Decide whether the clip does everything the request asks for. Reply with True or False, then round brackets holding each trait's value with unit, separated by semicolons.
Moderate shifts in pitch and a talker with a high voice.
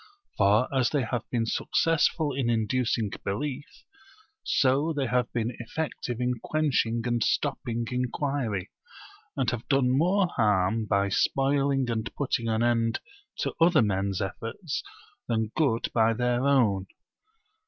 False (3.6 semitones; 120 Hz)